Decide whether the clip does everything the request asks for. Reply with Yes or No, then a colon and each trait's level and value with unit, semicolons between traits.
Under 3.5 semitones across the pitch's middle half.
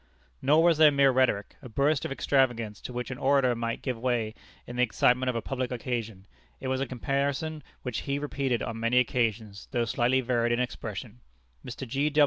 Yes: average, 2.8 semitones